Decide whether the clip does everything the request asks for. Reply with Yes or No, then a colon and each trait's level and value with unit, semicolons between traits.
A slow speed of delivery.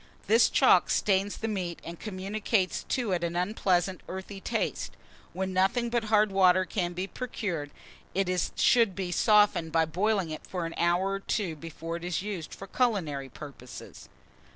No: average, 165 wpm